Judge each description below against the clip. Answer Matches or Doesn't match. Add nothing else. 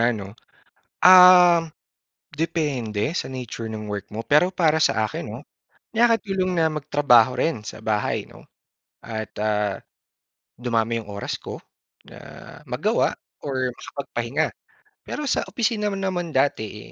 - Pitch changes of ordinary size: Doesn't match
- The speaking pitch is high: Doesn't match